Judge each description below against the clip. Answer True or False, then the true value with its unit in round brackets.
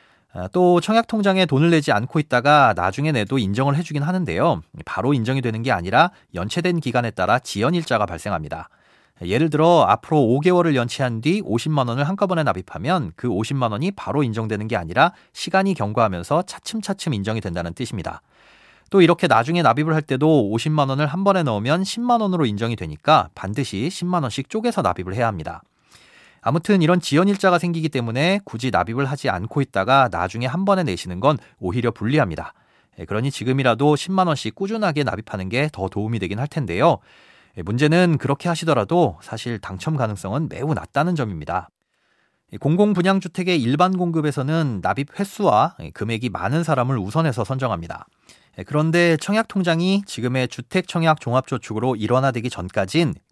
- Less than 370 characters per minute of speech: False (380 characters per minute)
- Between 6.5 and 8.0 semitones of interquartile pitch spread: True (6.9 semitones)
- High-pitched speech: False (140 Hz)